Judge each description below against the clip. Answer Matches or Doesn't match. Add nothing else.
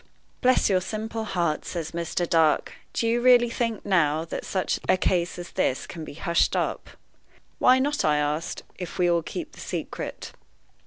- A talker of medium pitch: Matches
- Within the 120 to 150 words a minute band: Doesn't match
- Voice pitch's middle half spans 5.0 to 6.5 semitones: Matches